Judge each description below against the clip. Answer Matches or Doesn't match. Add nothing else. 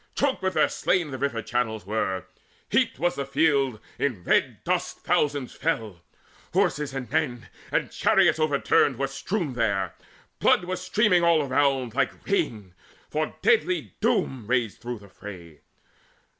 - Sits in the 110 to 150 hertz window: Matches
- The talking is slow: Doesn't match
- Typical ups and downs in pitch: Doesn't match